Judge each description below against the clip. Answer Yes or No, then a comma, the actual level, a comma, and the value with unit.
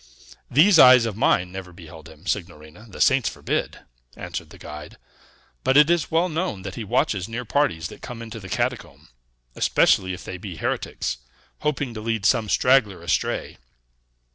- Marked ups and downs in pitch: Yes, wide, 6.1 semitones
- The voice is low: Yes, low, 105 Hz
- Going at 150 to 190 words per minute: Yes, average, 165 wpm